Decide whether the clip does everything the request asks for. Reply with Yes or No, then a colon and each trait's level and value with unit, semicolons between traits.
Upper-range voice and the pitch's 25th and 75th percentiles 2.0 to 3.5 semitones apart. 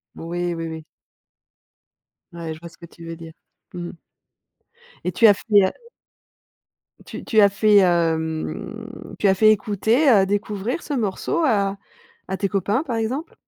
No: high, 195 Hz; average, 4.1 semitones